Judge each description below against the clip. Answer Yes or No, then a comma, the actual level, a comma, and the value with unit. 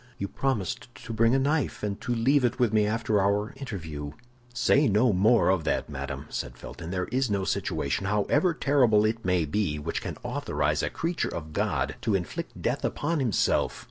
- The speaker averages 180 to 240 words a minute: Yes, average, 190 wpm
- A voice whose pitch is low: Yes, low, 105 Hz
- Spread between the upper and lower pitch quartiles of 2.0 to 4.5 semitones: No, wide, 5.4 semitones